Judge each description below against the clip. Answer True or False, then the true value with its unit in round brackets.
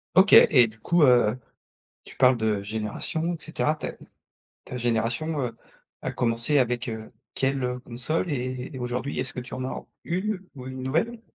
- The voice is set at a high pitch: False (130 Hz)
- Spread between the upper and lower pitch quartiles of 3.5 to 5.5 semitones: True (4.3 semitones)